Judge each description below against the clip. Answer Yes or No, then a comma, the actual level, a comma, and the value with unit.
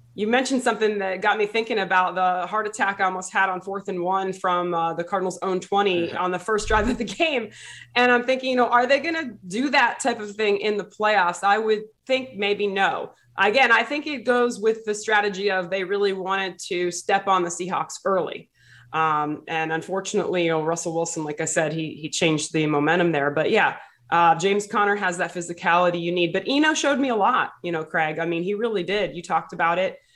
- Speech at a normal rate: No, fast, 230 wpm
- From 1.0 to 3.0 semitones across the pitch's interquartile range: No, average, 3.9 semitones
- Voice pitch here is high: Yes, high, 195 Hz